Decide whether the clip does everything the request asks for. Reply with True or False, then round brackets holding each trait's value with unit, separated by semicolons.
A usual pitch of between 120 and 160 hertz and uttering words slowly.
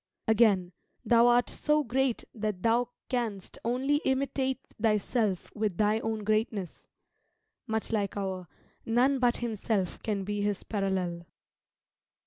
False (220 Hz; 120 wpm)